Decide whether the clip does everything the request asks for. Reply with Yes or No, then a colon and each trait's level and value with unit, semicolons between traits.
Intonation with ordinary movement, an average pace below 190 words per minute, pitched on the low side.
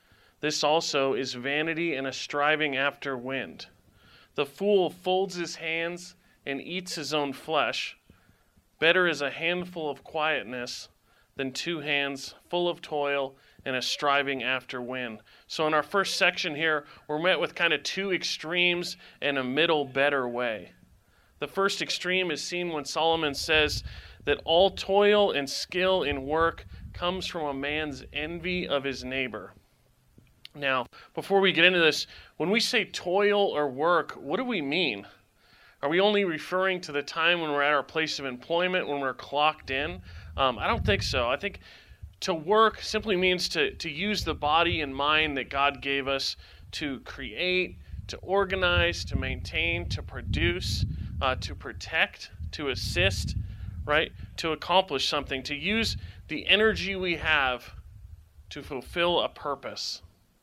No: average, 5.0 semitones; average, 160 wpm; medium, 150 Hz